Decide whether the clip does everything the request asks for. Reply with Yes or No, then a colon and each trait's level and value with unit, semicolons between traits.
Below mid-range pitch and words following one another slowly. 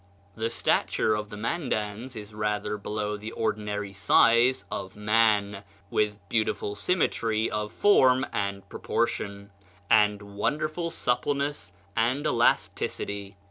Yes: low, 105 Hz; slow, 110 wpm